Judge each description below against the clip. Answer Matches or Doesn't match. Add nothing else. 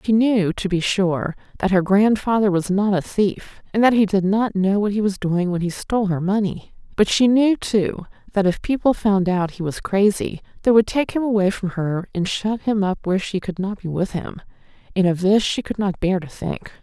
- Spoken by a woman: Matches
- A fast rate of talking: Matches